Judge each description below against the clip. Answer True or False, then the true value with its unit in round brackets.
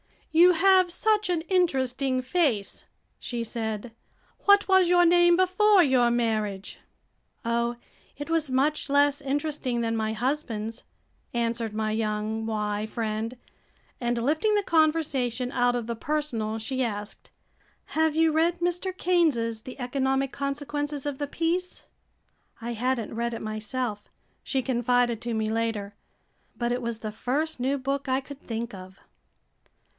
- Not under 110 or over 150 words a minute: True (145 wpm)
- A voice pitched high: True (255 Hz)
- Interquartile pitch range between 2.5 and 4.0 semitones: False (5.5 semitones)